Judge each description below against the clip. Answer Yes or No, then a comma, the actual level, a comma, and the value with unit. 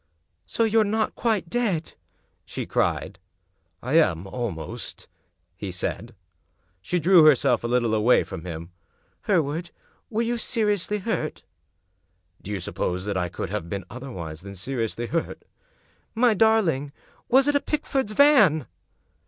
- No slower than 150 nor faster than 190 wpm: Yes, average, 155 wpm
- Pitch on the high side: No, low, 135 Hz